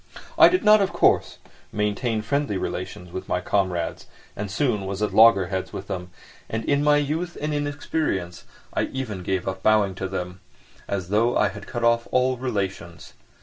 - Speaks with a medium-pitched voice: No, low, 105 Hz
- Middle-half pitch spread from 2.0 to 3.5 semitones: No, wide, 5.6 semitones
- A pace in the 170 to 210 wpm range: Yes, average, 175 wpm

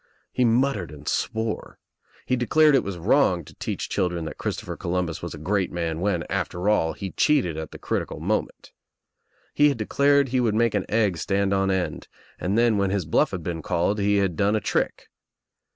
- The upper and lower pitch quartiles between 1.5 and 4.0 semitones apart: No, average, 4.8 semitones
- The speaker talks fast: Yes, fast, 210 wpm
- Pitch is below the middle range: Yes, low, 100 Hz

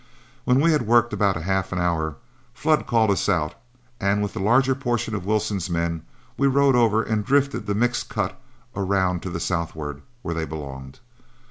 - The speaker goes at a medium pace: Yes, average, 180 wpm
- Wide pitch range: Yes, wide, 6.0 semitones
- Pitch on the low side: Yes, low, 100 Hz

